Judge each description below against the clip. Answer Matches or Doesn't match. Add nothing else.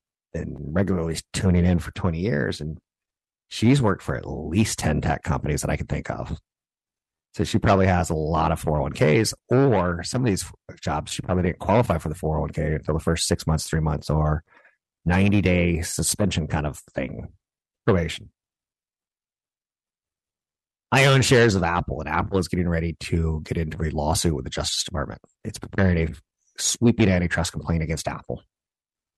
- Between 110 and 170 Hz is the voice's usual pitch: Doesn't match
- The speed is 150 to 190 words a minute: Matches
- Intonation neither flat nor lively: Matches